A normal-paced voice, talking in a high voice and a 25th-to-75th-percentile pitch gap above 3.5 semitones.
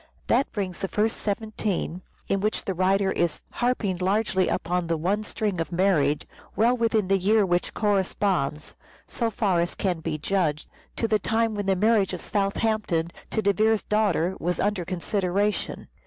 No: average, 170 wpm; high, 195 Hz; average, 3.1 semitones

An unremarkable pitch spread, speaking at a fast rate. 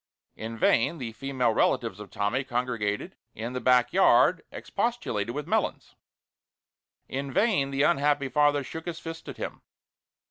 No: average, 3.9 semitones; average, 145 wpm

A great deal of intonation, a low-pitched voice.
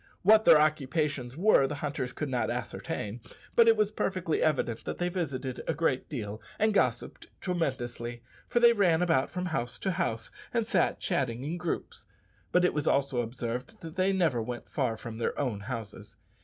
No: wide, 6.6 semitones; medium, 145 Hz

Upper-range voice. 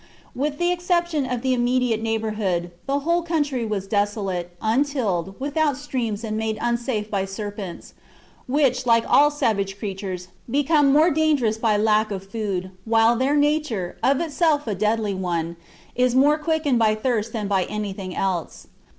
Yes: high, 230 Hz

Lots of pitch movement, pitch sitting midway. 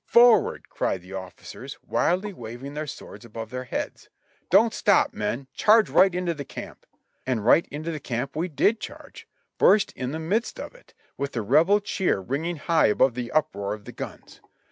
Yes: wide, 7.1 semitones; medium, 145 Hz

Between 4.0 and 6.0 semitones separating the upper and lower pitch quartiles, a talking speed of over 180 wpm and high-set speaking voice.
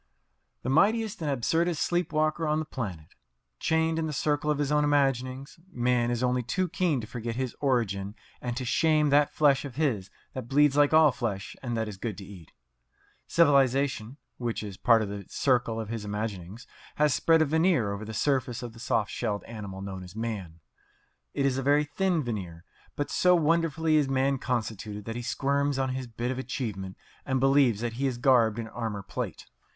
No: average, 4.8 semitones; average, 195 wpm; low, 130 Hz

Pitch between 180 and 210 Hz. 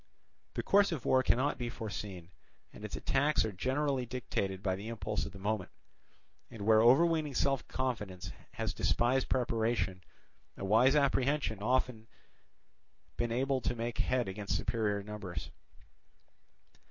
No: low, 115 Hz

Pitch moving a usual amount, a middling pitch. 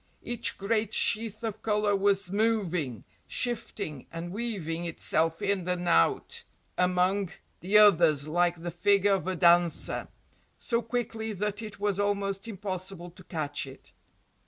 No: average, 3.4 semitones; high, 195 Hz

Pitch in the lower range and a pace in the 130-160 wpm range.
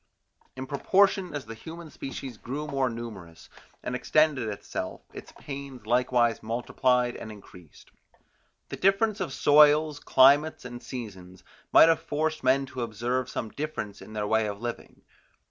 Yes: low, 130 Hz; average, 145 wpm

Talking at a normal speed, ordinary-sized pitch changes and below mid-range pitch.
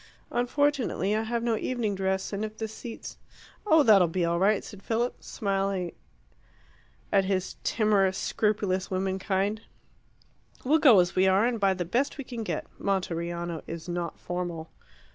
No: average, 160 wpm; average, 3.3 semitones; high, 195 Hz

